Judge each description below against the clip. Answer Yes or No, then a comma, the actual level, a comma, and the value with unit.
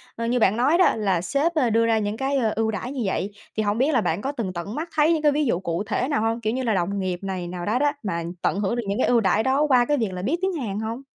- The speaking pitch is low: No, high, 225 Hz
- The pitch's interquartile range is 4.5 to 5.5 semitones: Yes, average, 5.1 semitones